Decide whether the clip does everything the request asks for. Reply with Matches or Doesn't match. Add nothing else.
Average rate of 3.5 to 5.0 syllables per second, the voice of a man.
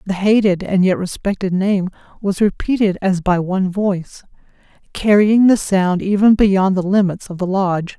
Doesn't match